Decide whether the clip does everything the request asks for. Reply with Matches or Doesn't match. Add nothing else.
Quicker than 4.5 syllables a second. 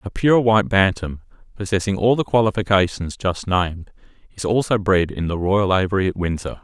Matches